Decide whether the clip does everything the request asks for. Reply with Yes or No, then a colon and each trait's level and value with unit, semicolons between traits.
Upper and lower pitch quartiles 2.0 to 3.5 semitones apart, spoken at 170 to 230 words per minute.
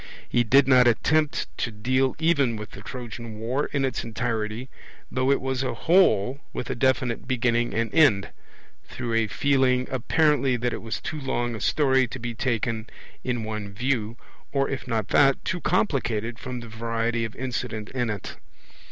Yes: average, 2.8 semitones; average, 180 wpm